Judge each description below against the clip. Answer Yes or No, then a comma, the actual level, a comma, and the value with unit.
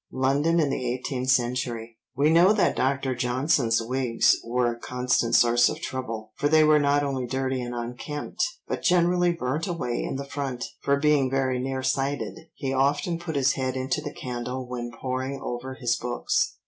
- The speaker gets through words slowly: No, average, 175 wpm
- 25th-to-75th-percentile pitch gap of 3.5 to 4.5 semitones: No, narrow, 2.6 semitones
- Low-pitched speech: Yes, low, 130 Hz